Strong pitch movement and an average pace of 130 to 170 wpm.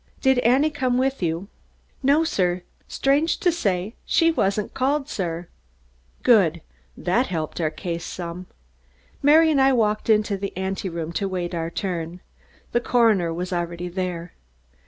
Yes: wide, 6.9 semitones; average, 145 wpm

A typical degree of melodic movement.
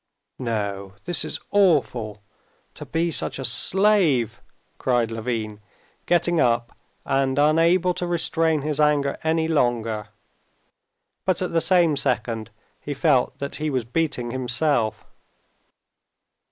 No: wide, 5.7 semitones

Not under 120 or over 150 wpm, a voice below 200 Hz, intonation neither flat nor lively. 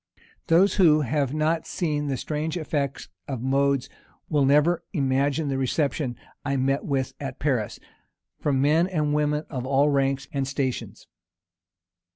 No: average, 145 wpm; medium, 140 Hz; narrow, 2.1 semitones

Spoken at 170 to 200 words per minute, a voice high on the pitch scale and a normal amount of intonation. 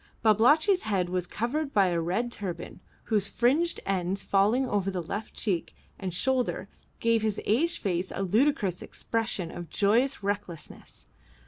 No: average, 150 wpm; high, 205 Hz; average, 4.6 semitones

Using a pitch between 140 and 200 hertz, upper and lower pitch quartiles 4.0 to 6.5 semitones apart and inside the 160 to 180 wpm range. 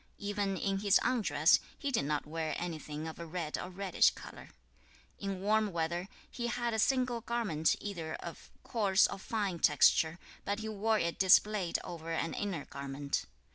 Yes: high, 190 Hz; average, 4.7 semitones; average, 175 wpm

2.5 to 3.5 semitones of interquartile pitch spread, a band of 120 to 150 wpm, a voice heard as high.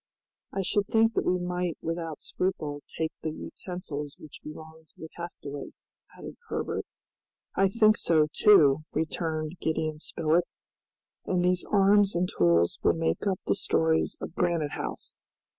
No: average, 2.8 semitones; average, 145 wpm; medium, 165 Hz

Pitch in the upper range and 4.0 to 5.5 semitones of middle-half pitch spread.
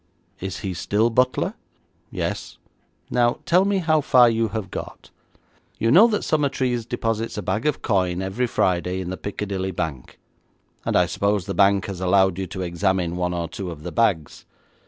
No: low, 100 Hz; average, 4.6 semitones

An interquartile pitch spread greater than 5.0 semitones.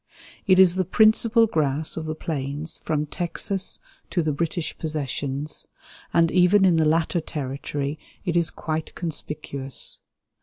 No: average, 3.2 semitones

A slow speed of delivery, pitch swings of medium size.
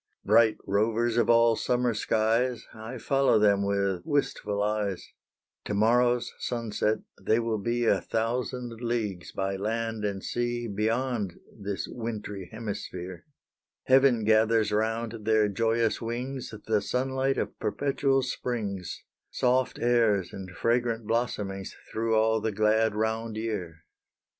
No: slow, 125 wpm; narrow, 2.3 semitones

